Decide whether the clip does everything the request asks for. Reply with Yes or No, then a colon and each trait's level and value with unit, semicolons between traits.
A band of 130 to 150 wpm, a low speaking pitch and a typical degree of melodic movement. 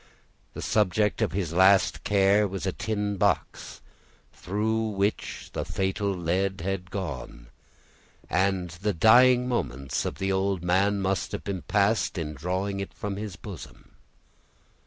No: slow, 135 wpm; very low, 95 Hz; narrow, 2.1 semitones